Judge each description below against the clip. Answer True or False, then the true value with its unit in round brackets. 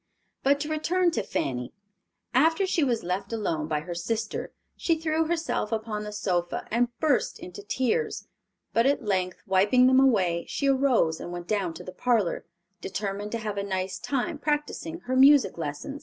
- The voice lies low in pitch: False (220 Hz)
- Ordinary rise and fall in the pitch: False (7.2 semitones)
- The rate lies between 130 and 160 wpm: False (175 wpm)